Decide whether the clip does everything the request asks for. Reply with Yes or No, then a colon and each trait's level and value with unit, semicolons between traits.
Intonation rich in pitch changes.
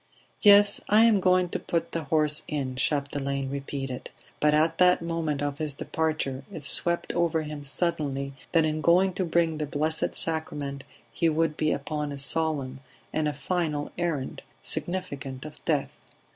No: average, 3.0 semitones